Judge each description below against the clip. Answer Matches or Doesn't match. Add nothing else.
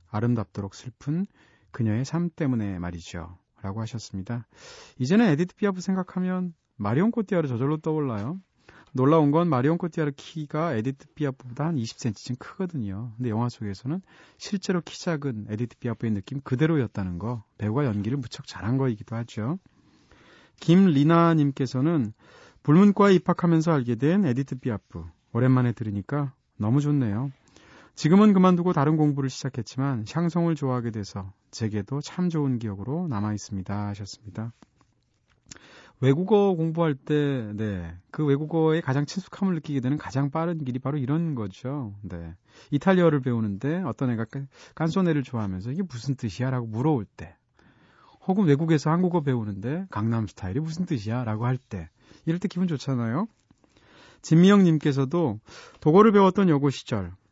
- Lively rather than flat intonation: Matches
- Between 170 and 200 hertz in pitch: Doesn't match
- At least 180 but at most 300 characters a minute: Doesn't match